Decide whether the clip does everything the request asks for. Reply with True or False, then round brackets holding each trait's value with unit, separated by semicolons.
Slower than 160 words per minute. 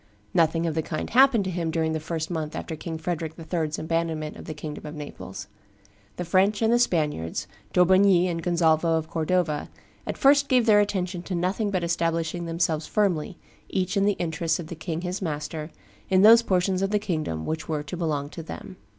False (200 wpm)